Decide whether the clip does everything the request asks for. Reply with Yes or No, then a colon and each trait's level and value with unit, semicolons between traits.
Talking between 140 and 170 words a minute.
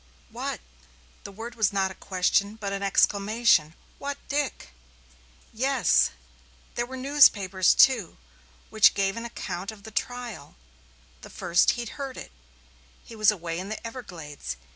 Yes: average, 150 wpm